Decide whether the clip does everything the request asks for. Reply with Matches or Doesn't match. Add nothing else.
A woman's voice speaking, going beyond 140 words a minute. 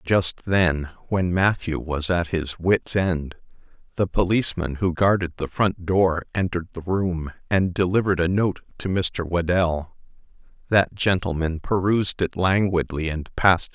Doesn't match